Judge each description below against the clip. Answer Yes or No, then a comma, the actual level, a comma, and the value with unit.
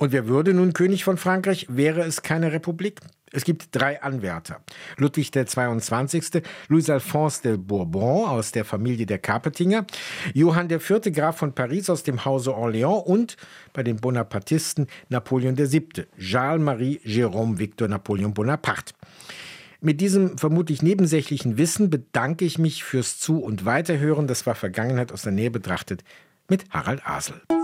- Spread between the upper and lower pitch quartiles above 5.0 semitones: Yes, wide, 5.6 semitones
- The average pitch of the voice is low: No, medium, 145 Hz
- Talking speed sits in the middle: Yes, average, 140 wpm